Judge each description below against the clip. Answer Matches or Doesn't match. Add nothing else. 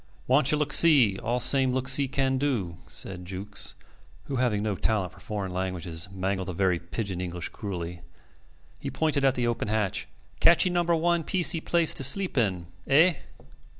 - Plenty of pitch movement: Matches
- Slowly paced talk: Doesn't match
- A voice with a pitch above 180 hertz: Doesn't match